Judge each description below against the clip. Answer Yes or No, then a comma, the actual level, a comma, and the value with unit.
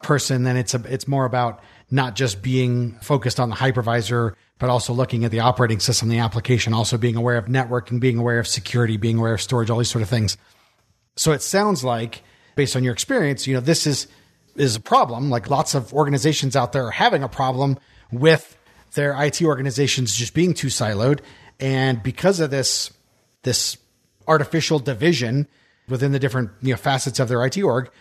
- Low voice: Yes, low, 130 Hz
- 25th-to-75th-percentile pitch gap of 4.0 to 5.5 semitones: No, average, 2.8 semitones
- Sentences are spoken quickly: No, average, 195 wpm